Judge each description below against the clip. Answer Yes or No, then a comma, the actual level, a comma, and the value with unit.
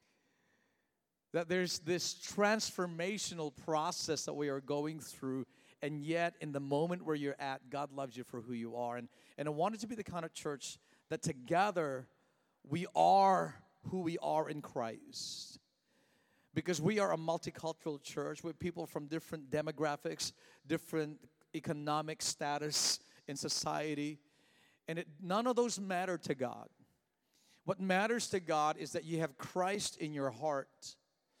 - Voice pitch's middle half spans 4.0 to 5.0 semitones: No, average, 3.5 semitones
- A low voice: No, medium, 160 Hz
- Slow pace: No, average, 155 wpm